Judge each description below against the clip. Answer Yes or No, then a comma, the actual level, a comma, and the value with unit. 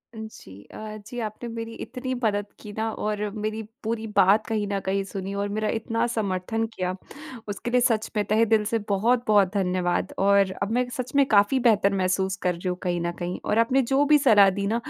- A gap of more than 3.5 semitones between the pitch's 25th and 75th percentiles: No, average, 2.7 semitones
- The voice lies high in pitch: Yes, high, 210 Hz